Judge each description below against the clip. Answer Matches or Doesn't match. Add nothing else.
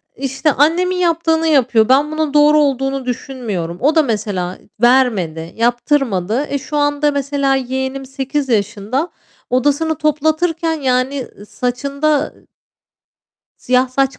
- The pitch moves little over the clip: Doesn't match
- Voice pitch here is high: Matches